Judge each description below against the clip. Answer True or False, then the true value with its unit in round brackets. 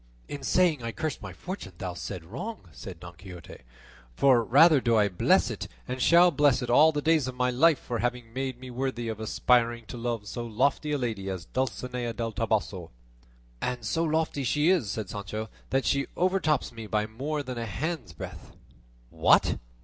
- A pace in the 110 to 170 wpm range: False (190 wpm)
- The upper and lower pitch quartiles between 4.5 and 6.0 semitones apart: True (5.0 semitones)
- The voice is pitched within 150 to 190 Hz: False (120 Hz)